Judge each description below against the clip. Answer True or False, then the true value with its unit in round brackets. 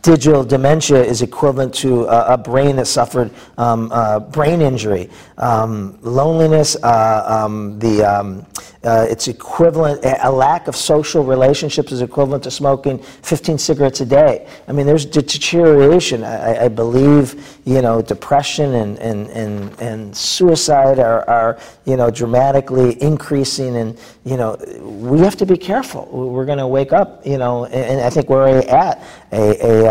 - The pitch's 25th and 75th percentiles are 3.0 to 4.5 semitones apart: True (4.0 semitones)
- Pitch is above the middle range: False (130 Hz)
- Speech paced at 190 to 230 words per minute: False (160 wpm)